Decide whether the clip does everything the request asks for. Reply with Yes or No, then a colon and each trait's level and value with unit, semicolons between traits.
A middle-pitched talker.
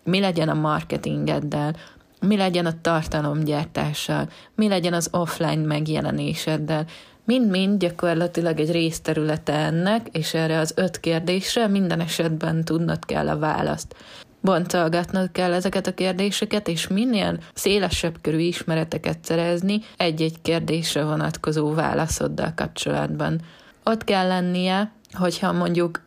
Yes: medium, 165 Hz